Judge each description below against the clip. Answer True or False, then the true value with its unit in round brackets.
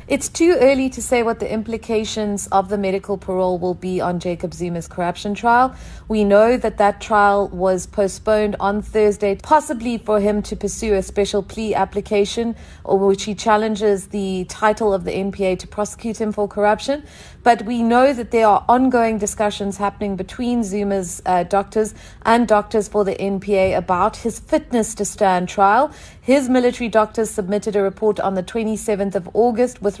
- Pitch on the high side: True (210 Hz)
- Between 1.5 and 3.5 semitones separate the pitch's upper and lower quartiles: True (2.4 semitones)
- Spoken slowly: False (175 wpm)